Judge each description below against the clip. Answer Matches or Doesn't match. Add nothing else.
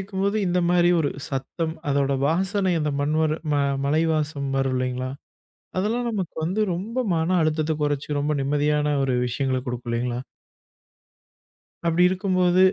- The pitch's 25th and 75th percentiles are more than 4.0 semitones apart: Matches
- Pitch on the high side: Doesn't match